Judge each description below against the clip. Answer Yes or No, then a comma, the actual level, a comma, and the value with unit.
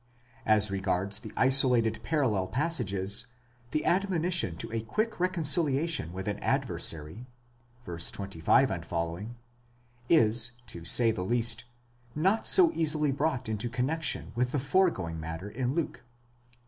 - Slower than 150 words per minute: Yes, slow, 135 wpm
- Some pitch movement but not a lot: No, wide, 7.4 semitones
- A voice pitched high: No, low, 120 Hz